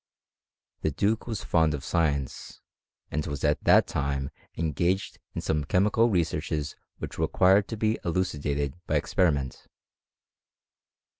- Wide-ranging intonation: No, average, 4.6 semitones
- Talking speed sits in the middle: No, slow, 130 wpm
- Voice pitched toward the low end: Yes, very low, 80 Hz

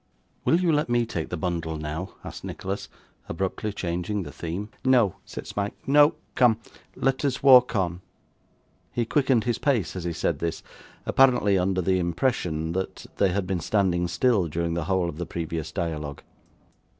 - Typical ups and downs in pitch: No, wide, 6.0 semitones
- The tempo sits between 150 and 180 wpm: Yes, average, 170 wpm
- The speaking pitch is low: Yes, very low, 95 Hz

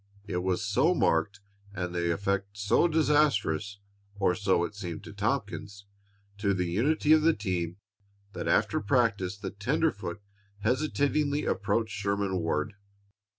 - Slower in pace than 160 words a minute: Yes, slow, 135 wpm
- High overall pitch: No, low, 100 Hz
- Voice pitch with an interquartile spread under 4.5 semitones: No, average, 5.0 semitones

